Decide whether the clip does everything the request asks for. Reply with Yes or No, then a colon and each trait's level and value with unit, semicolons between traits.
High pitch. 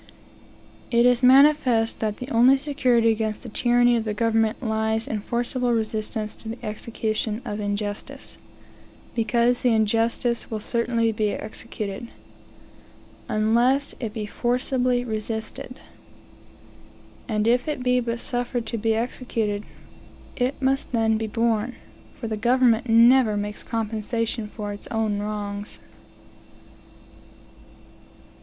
Yes: high, 230 Hz